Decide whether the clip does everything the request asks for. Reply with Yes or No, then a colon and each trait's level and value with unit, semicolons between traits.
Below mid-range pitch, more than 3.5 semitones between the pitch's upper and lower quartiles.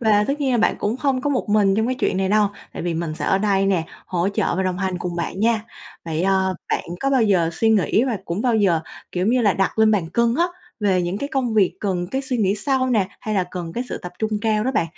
No: high, 205 Hz; average, 4.0 semitones